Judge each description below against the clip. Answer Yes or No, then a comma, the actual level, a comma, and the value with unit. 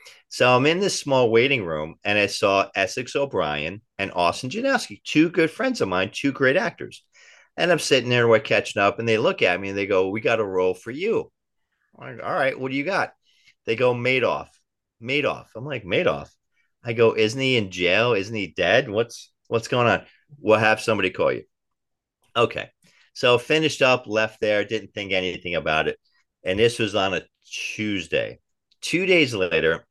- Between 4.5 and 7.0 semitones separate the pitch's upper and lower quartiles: Yes, average, 5.1 semitones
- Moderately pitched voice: No, low, 115 Hz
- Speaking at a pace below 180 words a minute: No, average, 200 wpm